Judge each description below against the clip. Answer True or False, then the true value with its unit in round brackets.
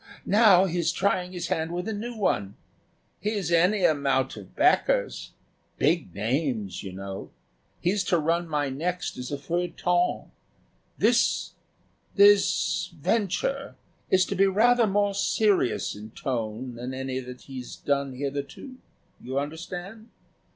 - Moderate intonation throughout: False (6.8 semitones)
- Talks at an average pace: False (130 wpm)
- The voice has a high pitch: False (170 Hz)